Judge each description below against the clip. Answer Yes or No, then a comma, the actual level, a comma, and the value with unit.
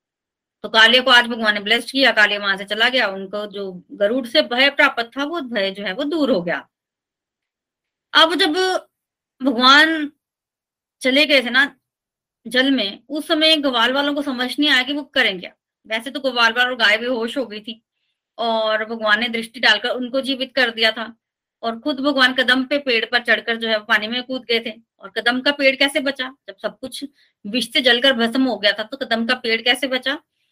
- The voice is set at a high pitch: Yes, very high, 250 Hz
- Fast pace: Yes, fast, 210 wpm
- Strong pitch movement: No, average, 3.6 semitones